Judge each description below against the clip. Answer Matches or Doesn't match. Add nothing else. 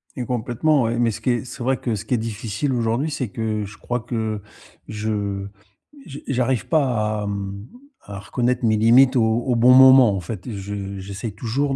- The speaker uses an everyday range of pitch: Matches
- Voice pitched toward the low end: Matches